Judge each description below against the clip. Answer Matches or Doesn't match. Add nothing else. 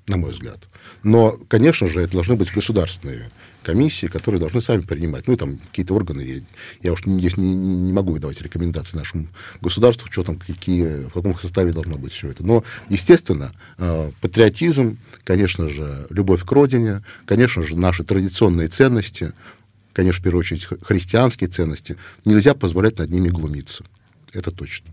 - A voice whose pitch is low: Matches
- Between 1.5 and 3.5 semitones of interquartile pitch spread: Doesn't match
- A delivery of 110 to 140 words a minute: Doesn't match